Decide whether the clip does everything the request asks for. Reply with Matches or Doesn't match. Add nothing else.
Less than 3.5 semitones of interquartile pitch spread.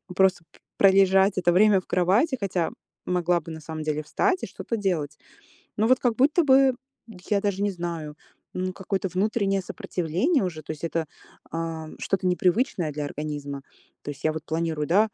Doesn't match